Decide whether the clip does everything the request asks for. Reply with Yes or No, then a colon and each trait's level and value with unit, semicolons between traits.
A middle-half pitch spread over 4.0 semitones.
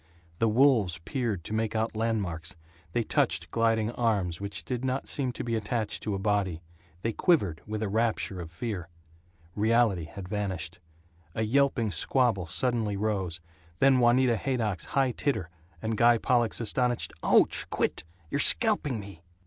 No: average, 3.7 semitones